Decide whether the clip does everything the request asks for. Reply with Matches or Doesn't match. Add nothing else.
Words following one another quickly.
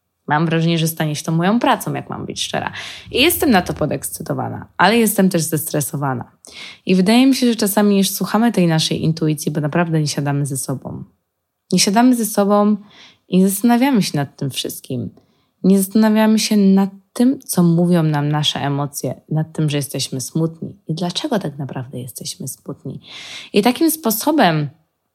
Matches